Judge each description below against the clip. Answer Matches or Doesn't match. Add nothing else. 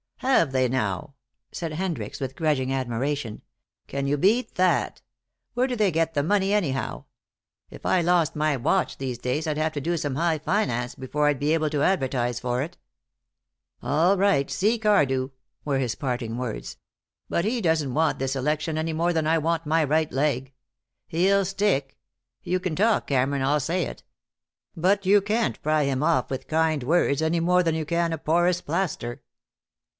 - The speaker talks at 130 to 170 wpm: Doesn't match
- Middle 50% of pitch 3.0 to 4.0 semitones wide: Doesn't match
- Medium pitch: Matches